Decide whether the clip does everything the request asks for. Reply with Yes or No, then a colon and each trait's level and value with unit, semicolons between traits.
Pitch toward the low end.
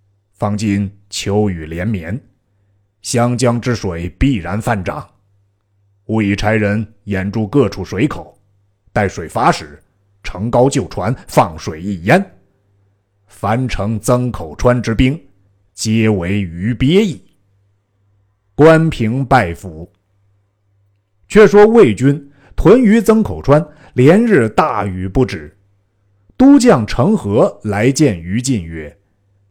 Yes: low, 100 Hz